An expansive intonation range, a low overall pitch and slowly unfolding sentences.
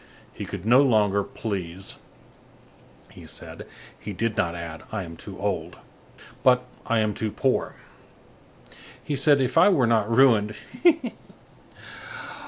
No: average, 4.9 semitones; low, 110 Hz; slow, 130 wpm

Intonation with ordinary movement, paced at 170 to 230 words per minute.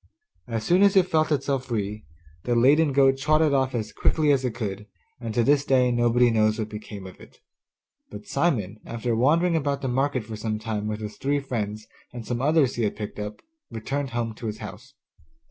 Yes: average, 4.4 semitones; fast, 205 wpm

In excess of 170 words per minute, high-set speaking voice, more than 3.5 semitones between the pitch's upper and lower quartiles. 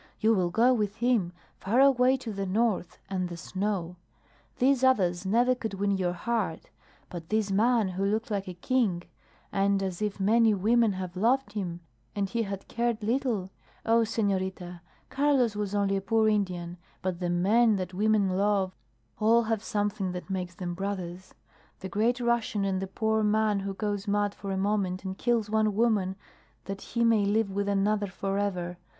No: average, 180 wpm; high, 200 Hz; average, 3.0 semitones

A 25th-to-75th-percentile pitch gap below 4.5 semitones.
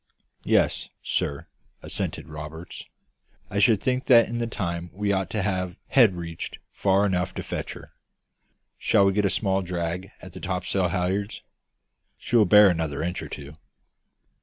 Yes: average, 2.9 semitones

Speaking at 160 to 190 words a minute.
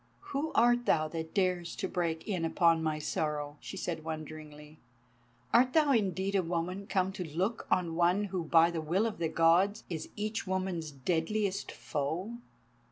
Yes: average, 165 wpm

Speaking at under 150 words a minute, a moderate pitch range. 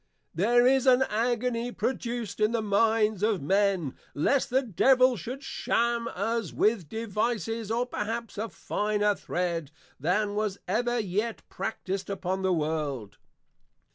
Yes: slow, 135 wpm; average, 3.7 semitones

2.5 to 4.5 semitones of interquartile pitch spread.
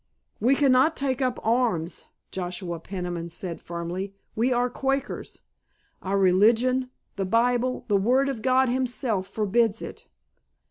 No: average, 5.3 semitones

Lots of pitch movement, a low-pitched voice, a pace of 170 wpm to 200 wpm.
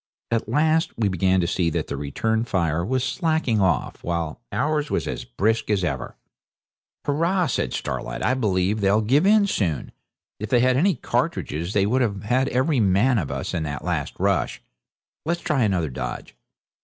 Yes: wide, 6.9 semitones; low, 110 Hz; average, 180 wpm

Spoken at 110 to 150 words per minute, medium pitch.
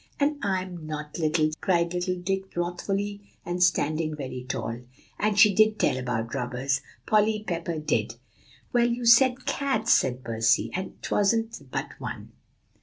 Yes: average, 145 wpm; medium, 180 Hz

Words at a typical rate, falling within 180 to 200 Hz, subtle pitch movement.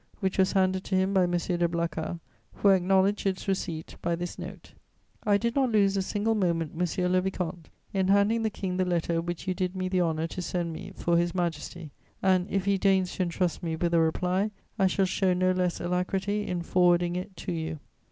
No: fast, 215 wpm; medium, 185 Hz; narrow, 1.8 semitones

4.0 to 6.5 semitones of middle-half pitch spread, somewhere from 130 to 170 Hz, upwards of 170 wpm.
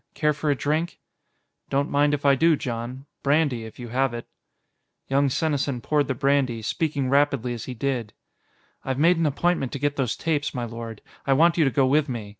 No: average, 3.0 semitones; medium, 140 Hz; fast, 205 wpm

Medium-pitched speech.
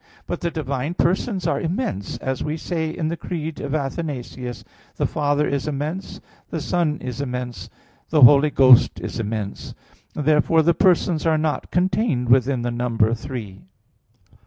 Yes: medium, 145 Hz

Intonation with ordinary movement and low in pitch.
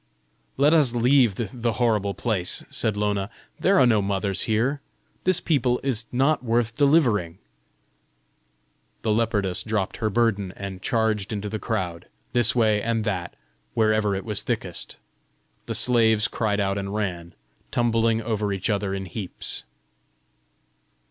Yes: average, 3.0 semitones; low, 110 Hz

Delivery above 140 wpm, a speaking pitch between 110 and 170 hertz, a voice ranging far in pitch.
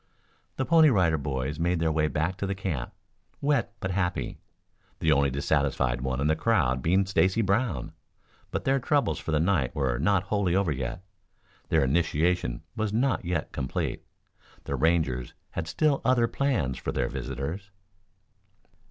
No: average, 160 wpm; very low, 85 Hz; wide, 6.1 semitones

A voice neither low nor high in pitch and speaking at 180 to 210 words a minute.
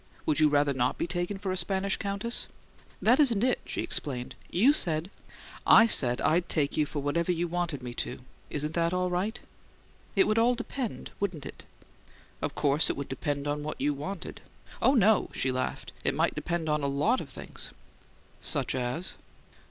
Yes: medium, 170 Hz; average, 190 wpm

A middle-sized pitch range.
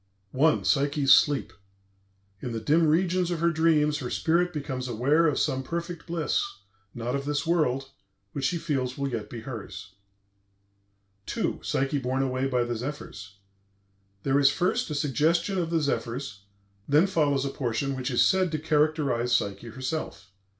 Yes: average, 4.2 semitones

